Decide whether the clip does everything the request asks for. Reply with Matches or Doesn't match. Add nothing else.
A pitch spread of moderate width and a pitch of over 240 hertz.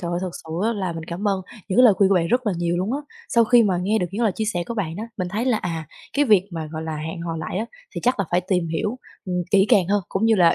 Doesn't match